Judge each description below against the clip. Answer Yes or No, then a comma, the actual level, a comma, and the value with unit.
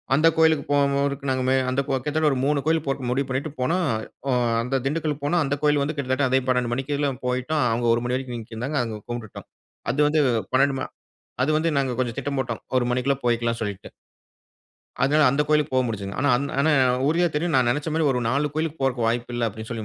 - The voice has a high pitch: No, low, 135 Hz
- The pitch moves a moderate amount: Yes, average, 3.3 semitones